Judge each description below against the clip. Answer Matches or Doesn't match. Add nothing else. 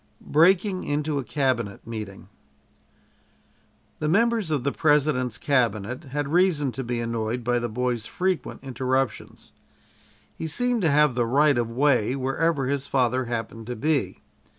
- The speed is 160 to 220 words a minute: Doesn't match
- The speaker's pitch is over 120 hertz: Matches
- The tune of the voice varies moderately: Matches